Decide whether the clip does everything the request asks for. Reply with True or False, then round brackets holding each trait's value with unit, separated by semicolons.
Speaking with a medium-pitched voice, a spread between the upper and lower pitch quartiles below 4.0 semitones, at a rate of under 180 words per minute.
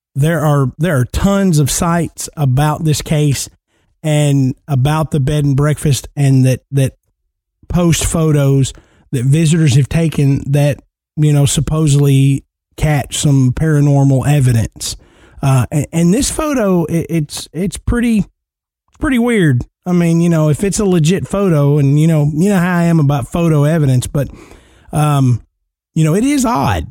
True (150 Hz; 3.4 semitones; 160 wpm)